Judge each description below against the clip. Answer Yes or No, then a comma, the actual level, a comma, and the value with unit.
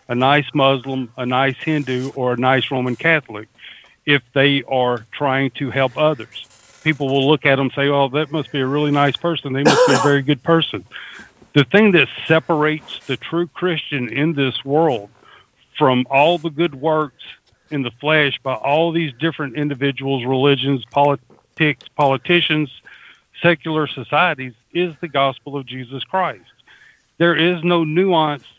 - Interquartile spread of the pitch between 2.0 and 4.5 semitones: Yes, average, 3.0 semitones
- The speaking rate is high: No, average, 165 wpm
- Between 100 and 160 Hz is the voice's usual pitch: Yes, medium, 140 Hz